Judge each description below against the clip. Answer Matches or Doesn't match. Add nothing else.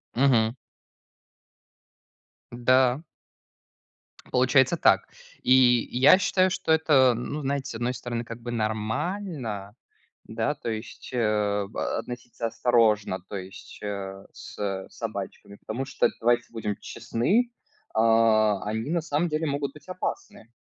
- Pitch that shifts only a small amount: Doesn't match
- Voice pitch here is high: Doesn't match